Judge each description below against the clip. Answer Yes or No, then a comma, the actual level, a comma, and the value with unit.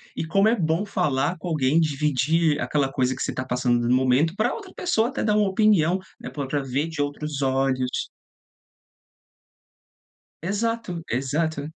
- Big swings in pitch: Yes, wide, 5.7 semitones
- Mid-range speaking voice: Yes, medium, 155 Hz